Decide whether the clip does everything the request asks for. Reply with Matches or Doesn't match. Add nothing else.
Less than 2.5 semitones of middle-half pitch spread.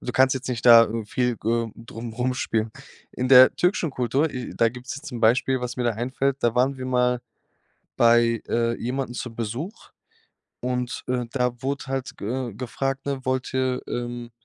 Matches